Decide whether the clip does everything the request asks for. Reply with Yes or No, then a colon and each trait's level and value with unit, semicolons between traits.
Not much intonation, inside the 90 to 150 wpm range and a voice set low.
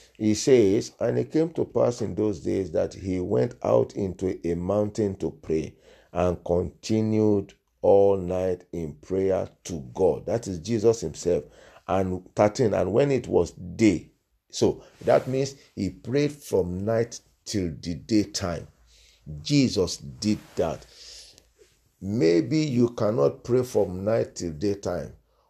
No: average, 4.3 semitones; average, 140 wpm; low, 100 Hz